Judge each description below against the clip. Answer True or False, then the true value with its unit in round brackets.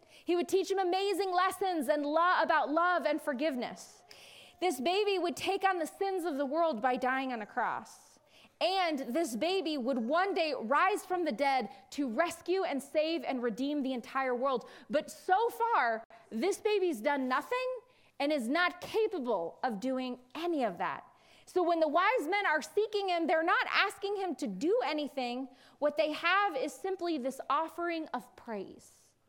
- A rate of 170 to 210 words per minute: True (180 wpm)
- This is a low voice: False (320 Hz)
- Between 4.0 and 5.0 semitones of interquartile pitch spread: False (5.5 semitones)